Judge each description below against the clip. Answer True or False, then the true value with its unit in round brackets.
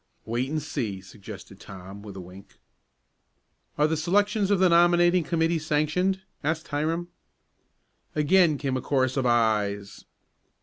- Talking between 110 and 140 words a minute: True (135 wpm)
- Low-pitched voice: False (150 Hz)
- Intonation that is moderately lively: False (7.9 semitones)